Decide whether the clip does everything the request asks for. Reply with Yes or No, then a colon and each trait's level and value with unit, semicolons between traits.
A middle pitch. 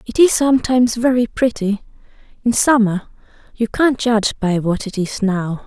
No: high, 225 Hz